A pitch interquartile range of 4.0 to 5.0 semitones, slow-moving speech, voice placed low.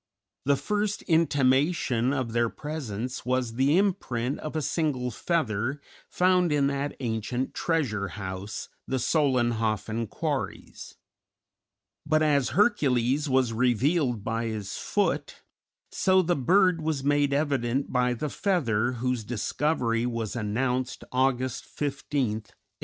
Yes: average, 4.4 semitones; slow, 120 wpm; low, 130 Hz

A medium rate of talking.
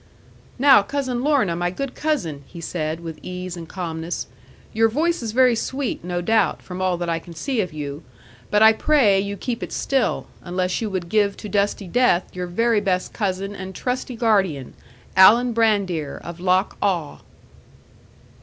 Yes: average, 175 wpm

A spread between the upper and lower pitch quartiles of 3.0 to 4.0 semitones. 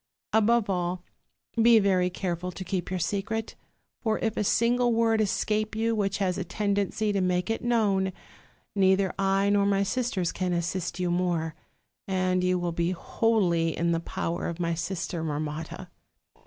Yes: average, 3.3 semitones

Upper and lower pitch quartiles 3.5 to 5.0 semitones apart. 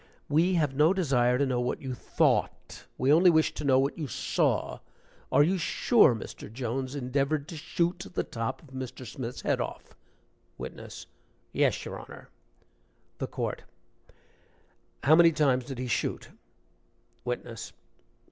Yes: average, 3.9 semitones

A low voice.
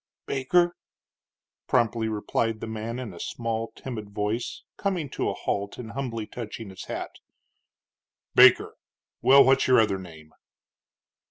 Yes: low, 115 Hz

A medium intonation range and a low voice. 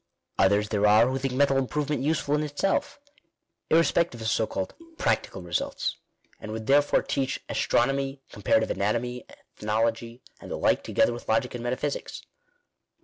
Yes: average, 4.0 semitones; low, 125 Hz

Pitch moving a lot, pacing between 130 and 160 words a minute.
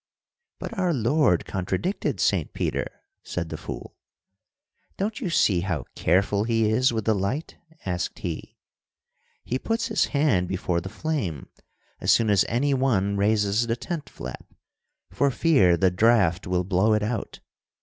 Yes: wide, 6.4 semitones; average, 150 wpm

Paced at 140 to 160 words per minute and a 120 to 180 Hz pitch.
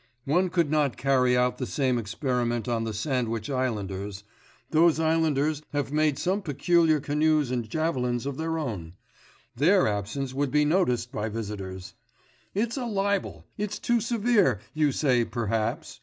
Yes: average, 150 wpm; low, 135 Hz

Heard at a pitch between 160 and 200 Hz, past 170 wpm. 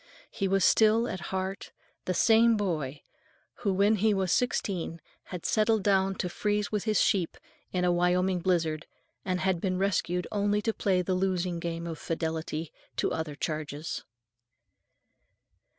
No: medium, 185 Hz; average, 150 wpm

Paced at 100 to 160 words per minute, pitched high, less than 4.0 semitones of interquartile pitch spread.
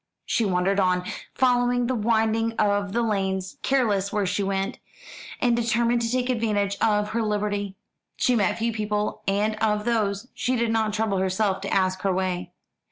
No: average, 170 wpm; high, 210 Hz; average, 2.8 semitones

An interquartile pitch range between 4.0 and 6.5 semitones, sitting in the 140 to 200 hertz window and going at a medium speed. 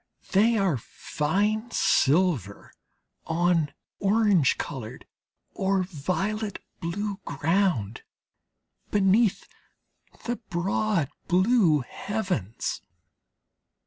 No: average, 5.1 semitones; medium, 185 Hz; slow, 70 wpm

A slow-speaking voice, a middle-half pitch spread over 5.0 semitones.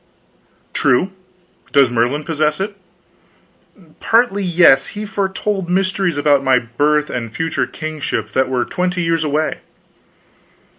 Yes: slow, 115 wpm; wide, 5.6 semitones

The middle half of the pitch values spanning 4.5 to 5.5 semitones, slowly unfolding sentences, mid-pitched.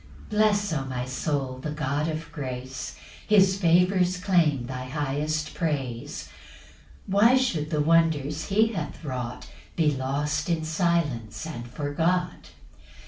Yes: average, 4.8 semitones; slow, 130 wpm; medium, 155 Hz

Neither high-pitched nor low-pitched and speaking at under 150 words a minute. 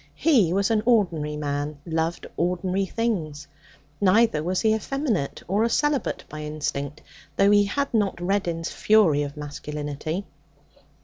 Yes: medium, 175 Hz; slow, 135 wpm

